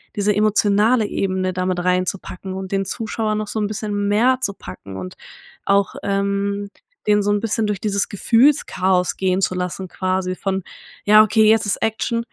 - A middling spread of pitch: No, narrow, 2.3 semitones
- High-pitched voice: Yes, high, 200 Hz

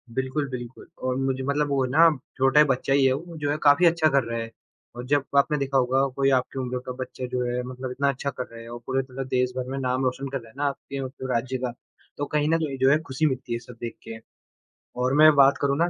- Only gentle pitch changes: Yes, narrow, 1.9 semitones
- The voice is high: No, low, 135 Hz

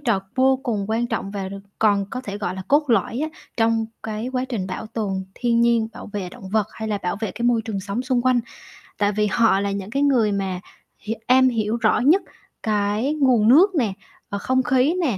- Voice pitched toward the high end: Yes, high, 225 Hz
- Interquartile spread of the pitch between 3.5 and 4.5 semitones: Yes, average, 3.8 semitones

